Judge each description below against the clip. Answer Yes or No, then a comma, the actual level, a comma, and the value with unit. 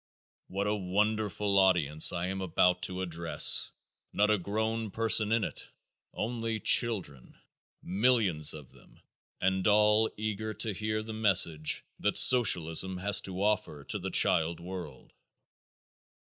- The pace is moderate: No, slow, 130 wpm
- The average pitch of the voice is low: Yes, low, 100 Hz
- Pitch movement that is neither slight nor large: Yes, average, 3.3 semitones